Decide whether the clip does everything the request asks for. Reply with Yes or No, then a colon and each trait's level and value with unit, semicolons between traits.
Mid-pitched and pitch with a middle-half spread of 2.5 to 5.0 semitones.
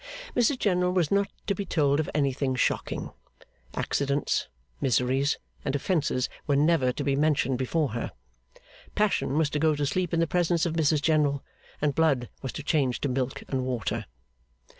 Yes: medium, 145 Hz; average, 3.5 semitones